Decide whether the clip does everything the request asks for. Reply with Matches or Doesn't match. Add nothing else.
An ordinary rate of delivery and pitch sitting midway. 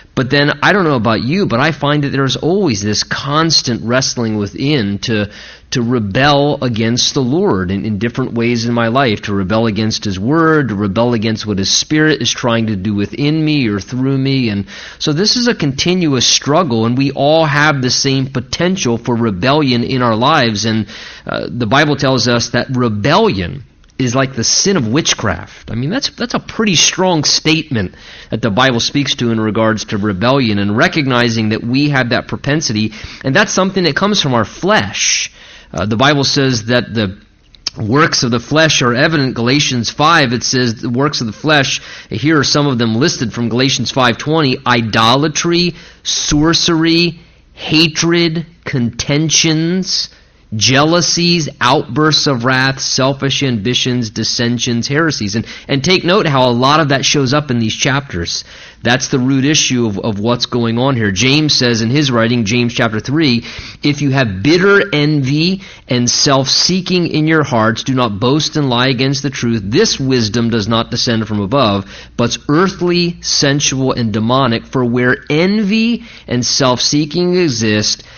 Doesn't match